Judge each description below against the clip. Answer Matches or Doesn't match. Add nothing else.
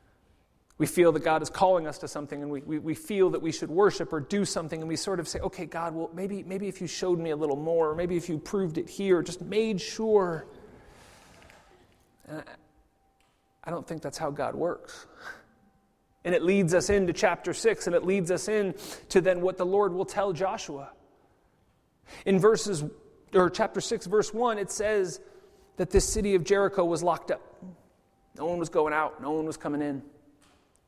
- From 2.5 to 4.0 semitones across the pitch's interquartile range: Matches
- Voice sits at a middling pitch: Matches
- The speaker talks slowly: Doesn't match